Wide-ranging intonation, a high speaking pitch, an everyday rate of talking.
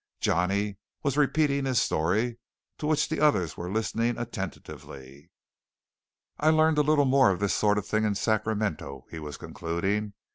No: wide, 7.3 semitones; low, 110 Hz; average, 155 wpm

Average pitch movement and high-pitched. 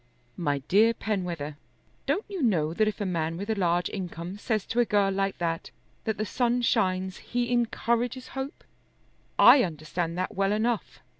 Yes: average, 5.0 semitones; high, 195 Hz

